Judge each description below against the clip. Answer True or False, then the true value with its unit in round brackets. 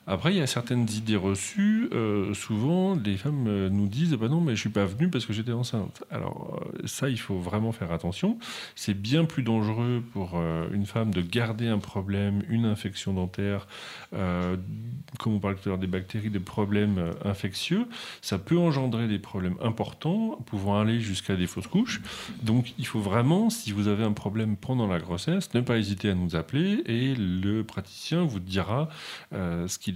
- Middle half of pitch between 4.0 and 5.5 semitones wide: True (4.7 semitones)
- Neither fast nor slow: True (195 wpm)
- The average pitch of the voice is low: True (110 Hz)